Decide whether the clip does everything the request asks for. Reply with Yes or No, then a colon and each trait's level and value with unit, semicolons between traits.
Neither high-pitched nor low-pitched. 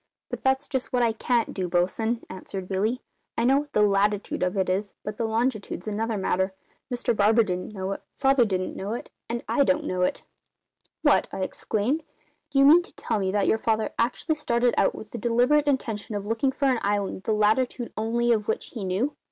No: high, 220 Hz